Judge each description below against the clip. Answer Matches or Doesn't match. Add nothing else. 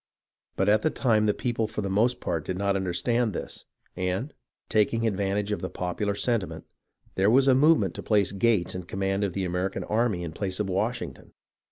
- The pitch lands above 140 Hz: Doesn't match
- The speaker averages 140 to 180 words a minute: Doesn't match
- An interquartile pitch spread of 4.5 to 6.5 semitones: Doesn't match